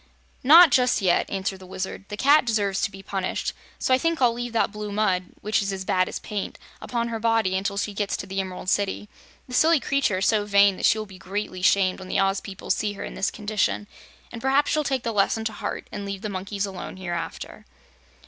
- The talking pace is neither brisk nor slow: No, fast, 235 wpm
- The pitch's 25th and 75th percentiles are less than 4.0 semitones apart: Yes, average, 3.2 semitones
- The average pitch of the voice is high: Yes, high, 205 Hz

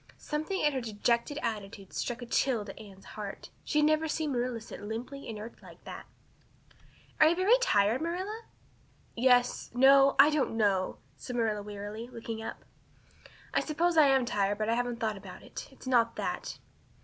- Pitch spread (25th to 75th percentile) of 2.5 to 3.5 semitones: No, average, 5.2 semitones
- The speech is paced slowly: No, average, 175 wpm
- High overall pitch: Yes, high, 240 Hz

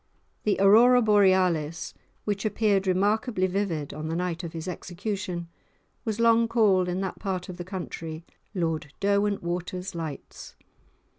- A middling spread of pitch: Yes, average, 3.1 semitones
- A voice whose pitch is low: No, medium, 185 Hz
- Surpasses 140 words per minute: No, slow, 135 wpm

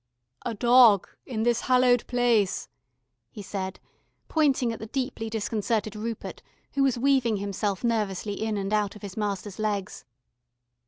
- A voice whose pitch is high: Yes, high, 220 Hz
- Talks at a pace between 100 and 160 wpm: Yes, average, 145 wpm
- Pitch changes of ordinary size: Yes, average, 3.1 semitones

